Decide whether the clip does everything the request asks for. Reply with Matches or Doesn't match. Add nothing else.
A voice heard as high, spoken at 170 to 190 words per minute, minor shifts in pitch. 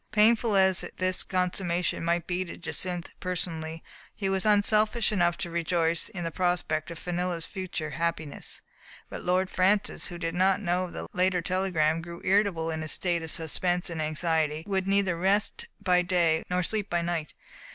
Doesn't match